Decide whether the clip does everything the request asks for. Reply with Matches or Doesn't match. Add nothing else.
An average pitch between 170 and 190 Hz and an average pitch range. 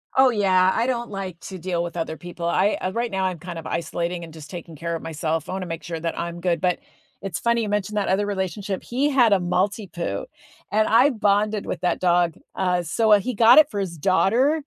Matches